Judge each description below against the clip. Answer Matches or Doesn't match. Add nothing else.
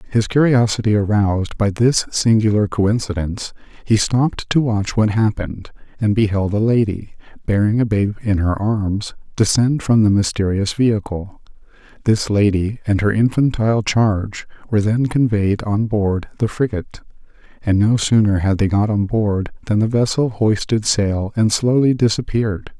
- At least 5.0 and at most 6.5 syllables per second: Doesn't match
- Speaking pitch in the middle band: Doesn't match